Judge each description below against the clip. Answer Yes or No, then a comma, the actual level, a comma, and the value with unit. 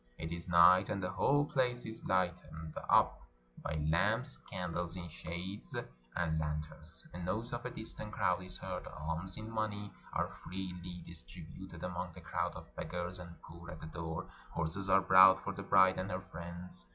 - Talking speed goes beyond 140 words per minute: Yes, average, 175 wpm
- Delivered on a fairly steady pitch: Yes, narrow, 2.3 semitones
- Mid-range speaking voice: No, very low, 90 Hz